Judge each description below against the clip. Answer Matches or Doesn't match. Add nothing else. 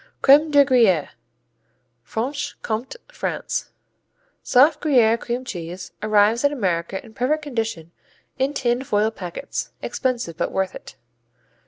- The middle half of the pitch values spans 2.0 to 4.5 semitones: Doesn't match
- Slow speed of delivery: Matches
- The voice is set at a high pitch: Matches